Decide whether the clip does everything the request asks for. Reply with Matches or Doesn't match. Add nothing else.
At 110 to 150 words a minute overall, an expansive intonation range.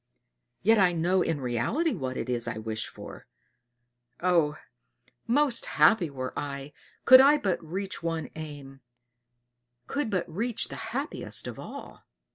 Matches